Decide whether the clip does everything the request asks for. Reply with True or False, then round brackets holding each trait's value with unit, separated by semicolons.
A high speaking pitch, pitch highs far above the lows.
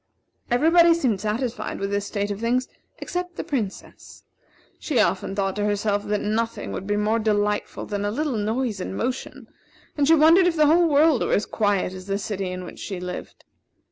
True (215 Hz; 5.7 semitones)